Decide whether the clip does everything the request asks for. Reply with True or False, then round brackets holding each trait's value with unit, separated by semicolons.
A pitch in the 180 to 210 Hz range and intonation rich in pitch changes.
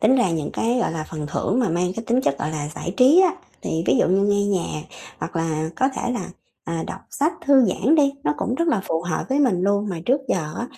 True (200 Hz; 7.8 semitones)